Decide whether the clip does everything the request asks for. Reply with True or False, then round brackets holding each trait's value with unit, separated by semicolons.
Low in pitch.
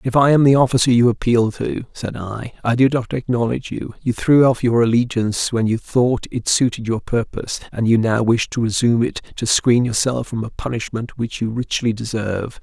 True (120 Hz)